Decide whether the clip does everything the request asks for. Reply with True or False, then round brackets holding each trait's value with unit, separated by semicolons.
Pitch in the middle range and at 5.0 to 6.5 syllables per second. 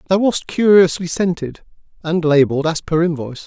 True (165 Hz; 5.5 syllables/s)